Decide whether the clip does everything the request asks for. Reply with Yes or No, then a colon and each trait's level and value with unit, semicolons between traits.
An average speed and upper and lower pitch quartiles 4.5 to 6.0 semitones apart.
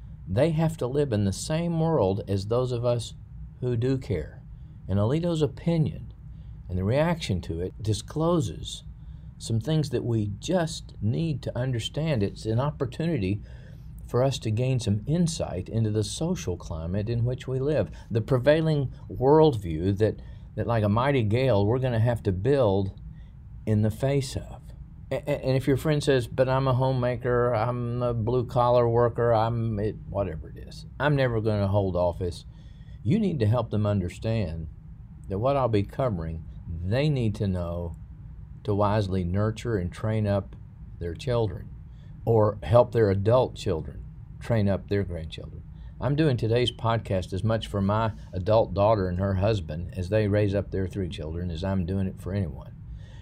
Yes: average, 170 wpm; average, 4.9 semitones